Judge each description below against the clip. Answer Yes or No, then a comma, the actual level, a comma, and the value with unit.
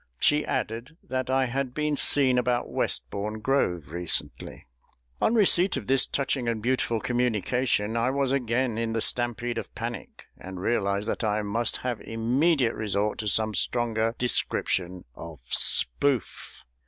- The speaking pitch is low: Yes, low, 120 Hz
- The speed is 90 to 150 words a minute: Yes, average, 145 wpm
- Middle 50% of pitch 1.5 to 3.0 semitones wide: No, average, 3.5 semitones